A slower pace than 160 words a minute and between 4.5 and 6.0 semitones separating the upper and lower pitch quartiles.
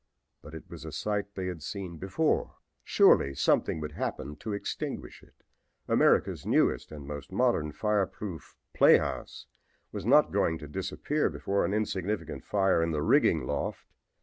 Yes: average, 150 wpm; average, 5.1 semitones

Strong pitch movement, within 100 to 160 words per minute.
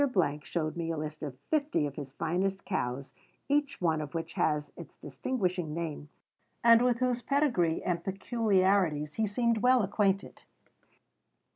Yes: wide, 6.9 semitones; average, 145 wpm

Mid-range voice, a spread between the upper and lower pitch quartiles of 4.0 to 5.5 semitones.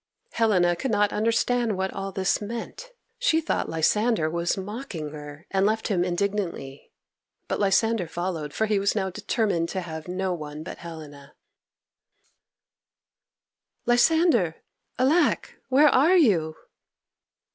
No: high, 195 Hz; average, 5.2 semitones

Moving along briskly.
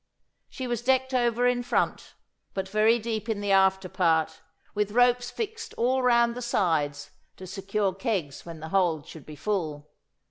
No: average, 170 wpm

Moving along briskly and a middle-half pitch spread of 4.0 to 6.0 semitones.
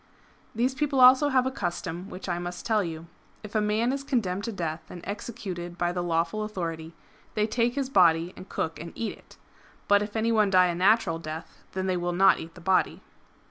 Yes: fast, 220 wpm; average, 4.5 semitones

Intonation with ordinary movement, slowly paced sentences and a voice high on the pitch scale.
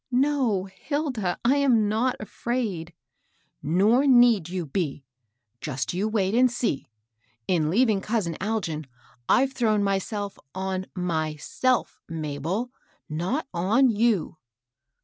No: wide, 5.8 semitones; slow, 125 wpm; high, 205 Hz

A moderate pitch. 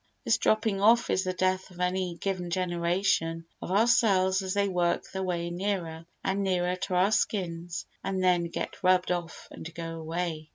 Yes: medium, 180 Hz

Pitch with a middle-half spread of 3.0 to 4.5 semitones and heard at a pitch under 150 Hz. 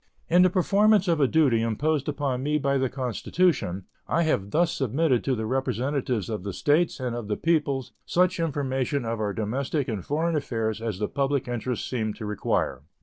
No: average, 5.2 semitones; low, 135 Hz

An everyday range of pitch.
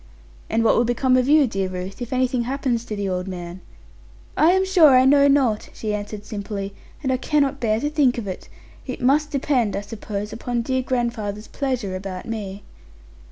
Yes: average, 4.5 semitones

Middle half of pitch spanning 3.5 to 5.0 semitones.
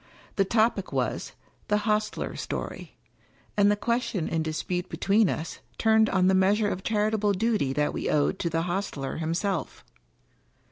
Yes: average, 3.9 semitones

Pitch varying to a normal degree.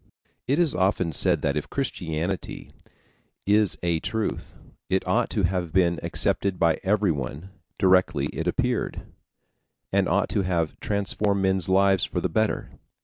Yes: average, 3.1 semitones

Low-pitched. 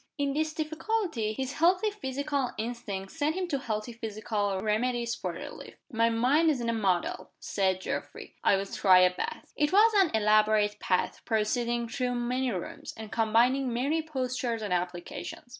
No: high, 235 Hz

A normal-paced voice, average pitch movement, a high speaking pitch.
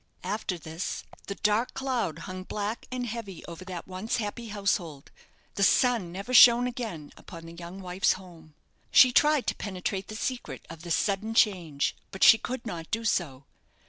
Yes: average, 175 wpm; average, 5.0 semitones; high, 195 Hz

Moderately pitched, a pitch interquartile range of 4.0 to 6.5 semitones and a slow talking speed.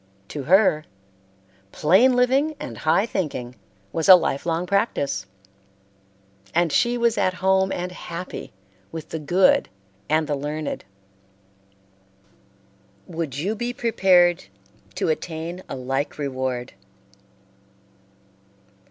Yes: medium, 175 Hz; average, 4.4 semitones; slow, 110 wpm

